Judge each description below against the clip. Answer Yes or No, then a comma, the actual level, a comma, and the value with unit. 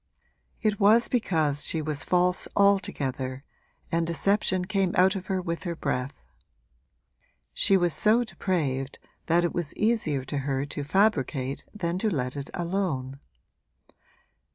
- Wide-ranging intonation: Yes, wide, 5.7 semitones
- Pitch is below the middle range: No, medium, 170 Hz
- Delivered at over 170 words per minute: No, slow, 135 wpm